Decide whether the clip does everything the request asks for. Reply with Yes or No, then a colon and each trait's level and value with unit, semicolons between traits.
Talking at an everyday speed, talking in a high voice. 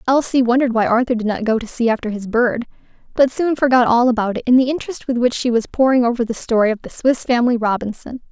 No: fast, 245 wpm; high, 240 Hz